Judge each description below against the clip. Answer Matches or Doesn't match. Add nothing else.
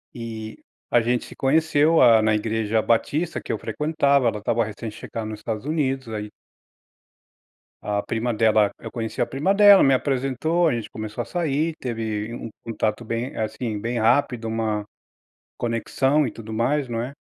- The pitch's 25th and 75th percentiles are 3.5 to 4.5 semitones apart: Matches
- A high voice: Doesn't match